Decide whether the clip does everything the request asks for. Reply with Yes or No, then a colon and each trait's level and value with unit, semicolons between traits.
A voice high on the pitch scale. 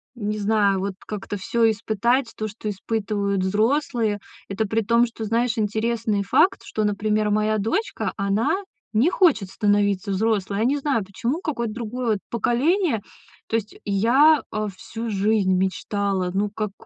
Yes: high, 215 Hz